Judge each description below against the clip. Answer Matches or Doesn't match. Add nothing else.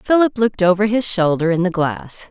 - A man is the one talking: Doesn't match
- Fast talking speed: Matches